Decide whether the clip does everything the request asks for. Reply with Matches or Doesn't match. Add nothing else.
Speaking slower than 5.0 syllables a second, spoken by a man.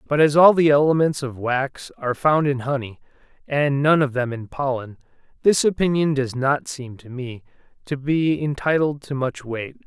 Matches